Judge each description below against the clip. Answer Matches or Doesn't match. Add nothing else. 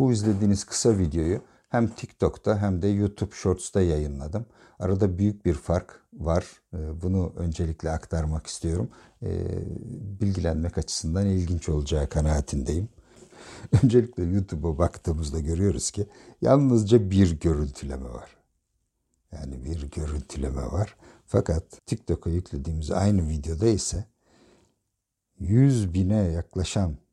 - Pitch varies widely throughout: Doesn't match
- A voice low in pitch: Matches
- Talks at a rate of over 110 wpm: Doesn't match